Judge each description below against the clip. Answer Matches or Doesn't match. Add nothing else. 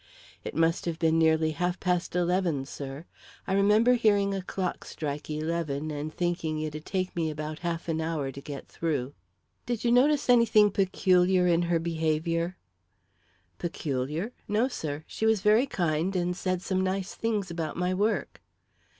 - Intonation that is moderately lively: Matches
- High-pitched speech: Doesn't match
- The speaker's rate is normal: Matches